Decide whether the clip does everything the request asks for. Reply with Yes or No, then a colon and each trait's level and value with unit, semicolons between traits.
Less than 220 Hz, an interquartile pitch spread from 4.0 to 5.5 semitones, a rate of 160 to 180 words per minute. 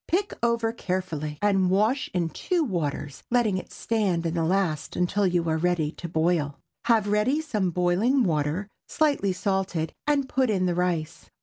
Yes: medium, 185 Hz; average, 5.2 semitones; average, 170 wpm